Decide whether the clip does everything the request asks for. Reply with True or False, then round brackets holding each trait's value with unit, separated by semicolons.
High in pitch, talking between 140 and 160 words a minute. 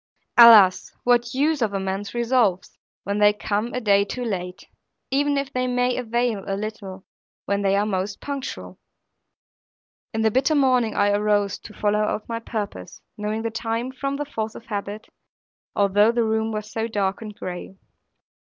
False (220 Hz; 170 wpm)